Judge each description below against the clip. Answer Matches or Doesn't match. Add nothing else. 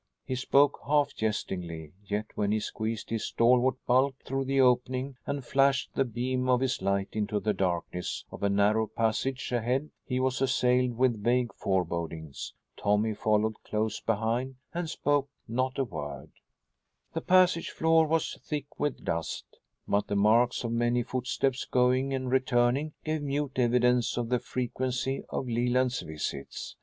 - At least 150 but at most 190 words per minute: Matches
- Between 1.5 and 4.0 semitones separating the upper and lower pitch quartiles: Matches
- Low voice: Matches